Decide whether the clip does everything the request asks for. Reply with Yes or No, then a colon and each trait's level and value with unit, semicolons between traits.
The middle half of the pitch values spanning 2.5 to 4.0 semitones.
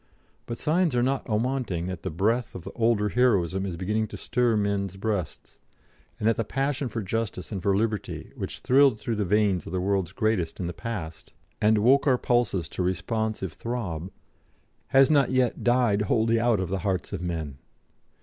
No: average, 4.4 semitones